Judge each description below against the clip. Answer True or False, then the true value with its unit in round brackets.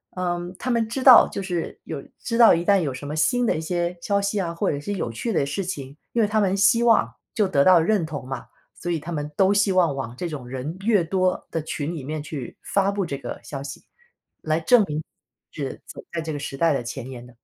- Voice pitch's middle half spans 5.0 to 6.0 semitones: True (5.5 semitones)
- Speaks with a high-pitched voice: False (170 Hz)